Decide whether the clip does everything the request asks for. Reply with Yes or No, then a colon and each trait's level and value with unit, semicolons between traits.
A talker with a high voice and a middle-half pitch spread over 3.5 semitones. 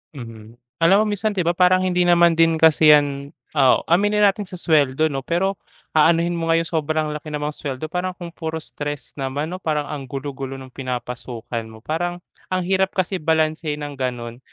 No: medium, 155 Hz; average, 4.1 semitones